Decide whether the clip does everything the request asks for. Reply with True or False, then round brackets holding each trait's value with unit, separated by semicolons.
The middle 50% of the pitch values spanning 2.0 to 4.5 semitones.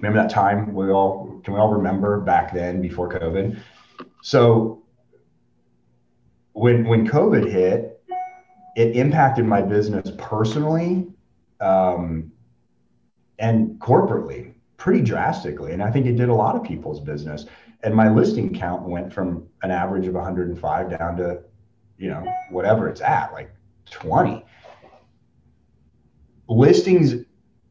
False (5.0 semitones)